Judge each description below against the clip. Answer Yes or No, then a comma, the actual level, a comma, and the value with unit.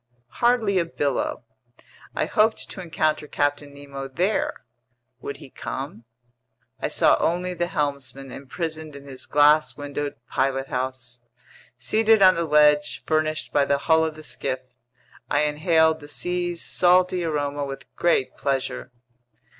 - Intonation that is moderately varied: Yes, average, 3.6 semitones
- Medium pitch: Yes, medium, 150 Hz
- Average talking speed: No, slow, 130 wpm